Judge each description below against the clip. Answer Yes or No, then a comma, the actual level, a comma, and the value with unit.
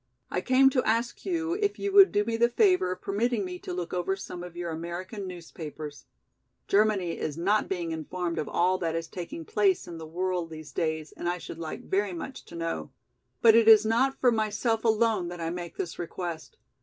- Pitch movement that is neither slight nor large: Yes, average, 4.9 semitones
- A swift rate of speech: Yes, fast, 210 wpm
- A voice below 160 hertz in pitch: No, medium, 185 Hz